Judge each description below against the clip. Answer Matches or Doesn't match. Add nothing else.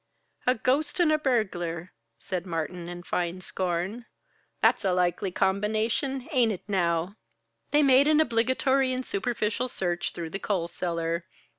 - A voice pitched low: Doesn't match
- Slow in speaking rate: Doesn't match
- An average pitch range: Doesn't match